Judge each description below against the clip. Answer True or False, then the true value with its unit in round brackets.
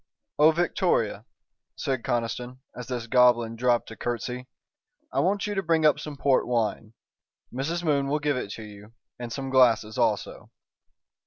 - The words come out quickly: False (160 wpm)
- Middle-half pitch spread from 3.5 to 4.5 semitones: True (4.1 semitones)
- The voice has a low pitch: True (125 Hz)